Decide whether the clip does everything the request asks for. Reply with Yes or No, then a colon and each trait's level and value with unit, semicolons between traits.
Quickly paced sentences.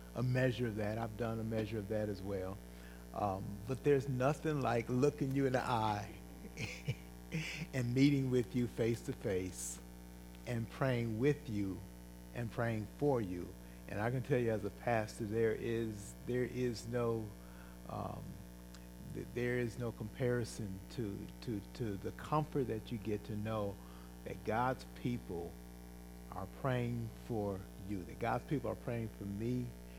No: average, 160 wpm